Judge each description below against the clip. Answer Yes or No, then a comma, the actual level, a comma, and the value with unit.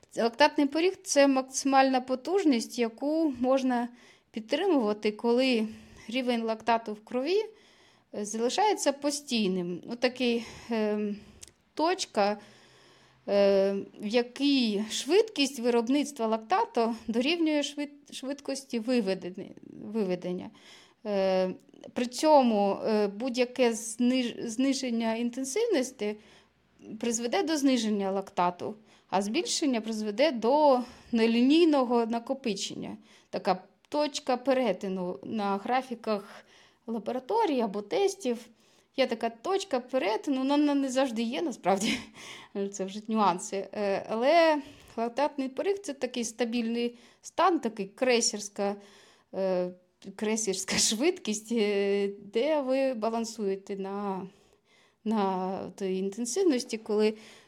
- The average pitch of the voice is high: Yes, high, 235 Hz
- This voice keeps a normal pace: No, slow, 90 wpm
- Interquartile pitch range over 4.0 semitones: Yes, average, 4.6 semitones